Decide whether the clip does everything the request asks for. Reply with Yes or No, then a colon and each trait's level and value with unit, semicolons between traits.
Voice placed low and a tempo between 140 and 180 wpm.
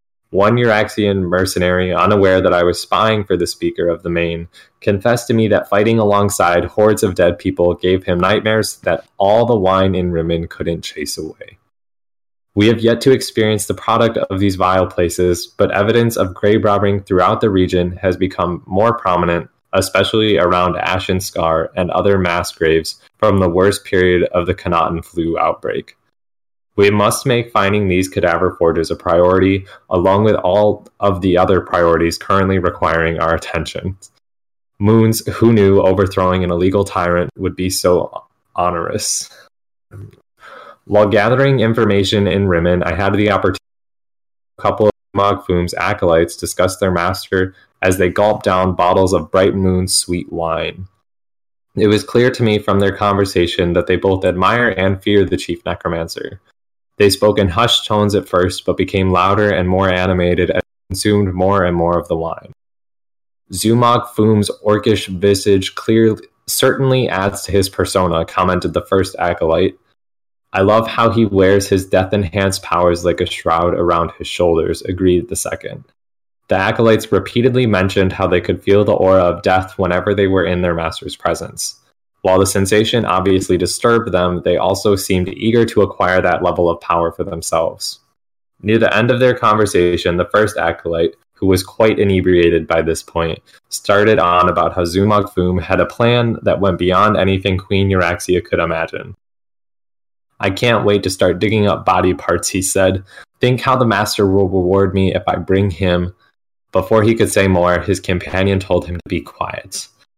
Yes: very low, 95 Hz; average, 170 wpm